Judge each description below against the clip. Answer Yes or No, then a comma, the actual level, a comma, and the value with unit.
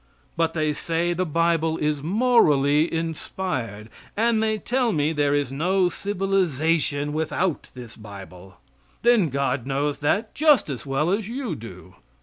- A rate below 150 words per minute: Yes, average, 140 wpm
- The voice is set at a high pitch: No, medium, 160 Hz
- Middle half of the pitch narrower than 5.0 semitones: No, average, 5.3 semitones